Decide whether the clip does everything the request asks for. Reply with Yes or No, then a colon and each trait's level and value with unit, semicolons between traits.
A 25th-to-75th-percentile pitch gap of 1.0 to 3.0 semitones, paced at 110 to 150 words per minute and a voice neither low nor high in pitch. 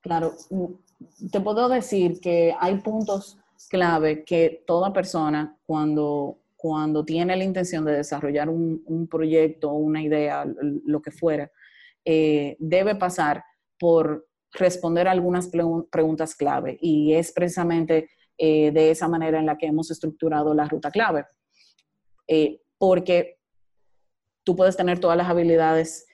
Yes: narrow, 2.6 semitones; average, 135 wpm; medium, 165 Hz